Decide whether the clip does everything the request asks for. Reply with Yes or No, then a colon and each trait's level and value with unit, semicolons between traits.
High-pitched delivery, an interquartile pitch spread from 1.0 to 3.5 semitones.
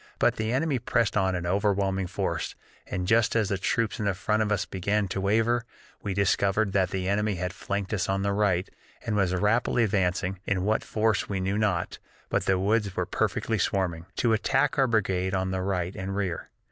No: low, 100 Hz; narrow, 2.4 semitones